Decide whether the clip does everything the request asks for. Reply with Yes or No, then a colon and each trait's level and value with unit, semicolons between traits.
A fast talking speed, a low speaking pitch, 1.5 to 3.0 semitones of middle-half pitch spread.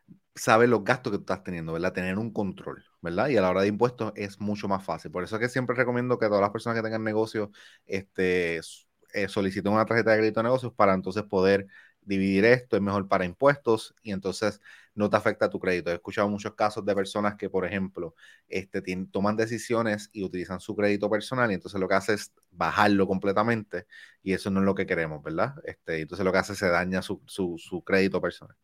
Yes: fast, 225 wpm; low, 100 Hz; average, 2.7 semitones